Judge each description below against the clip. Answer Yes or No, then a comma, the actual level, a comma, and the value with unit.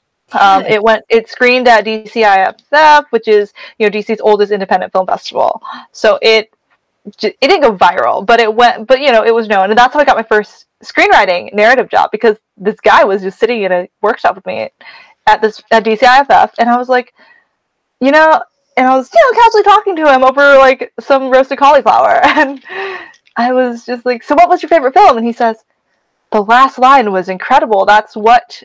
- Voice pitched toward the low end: No, high, 240 Hz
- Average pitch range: Yes, average, 4.3 semitones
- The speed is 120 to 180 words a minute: No, fast, 205 wpm